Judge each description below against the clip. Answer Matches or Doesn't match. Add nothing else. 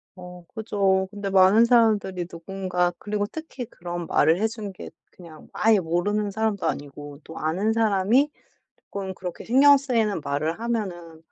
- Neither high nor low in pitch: Doesn't match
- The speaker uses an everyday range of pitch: Matches